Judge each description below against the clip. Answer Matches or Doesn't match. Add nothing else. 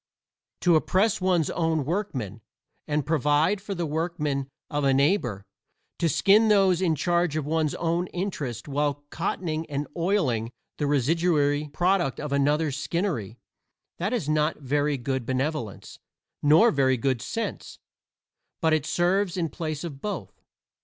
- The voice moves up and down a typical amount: Matches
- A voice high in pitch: Doesn't match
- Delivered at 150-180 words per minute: Doesn't match